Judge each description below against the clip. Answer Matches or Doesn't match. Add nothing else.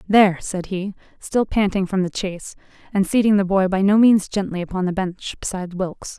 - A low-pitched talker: Doesn't match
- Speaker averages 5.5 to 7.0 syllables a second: Matches